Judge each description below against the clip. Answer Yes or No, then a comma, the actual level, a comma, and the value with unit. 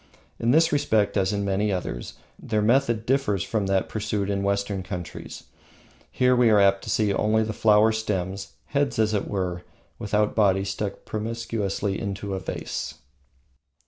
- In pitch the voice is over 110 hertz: No, low, 105 Hz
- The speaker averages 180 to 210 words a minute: No, average, 160 wpm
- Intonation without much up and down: Yes, narrow, 2.1 semitones